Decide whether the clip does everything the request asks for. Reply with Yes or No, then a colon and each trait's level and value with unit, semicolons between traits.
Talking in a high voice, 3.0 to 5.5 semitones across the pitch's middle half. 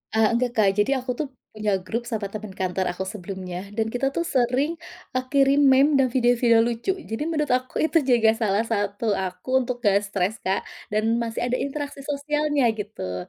Yes: high, 230 Hz; average, 4.8 semitones